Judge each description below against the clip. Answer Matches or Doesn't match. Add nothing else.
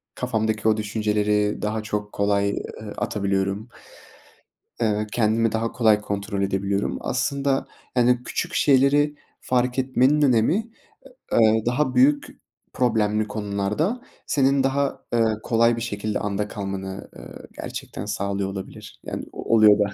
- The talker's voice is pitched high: Doesn't match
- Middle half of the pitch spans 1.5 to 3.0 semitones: Doesn't match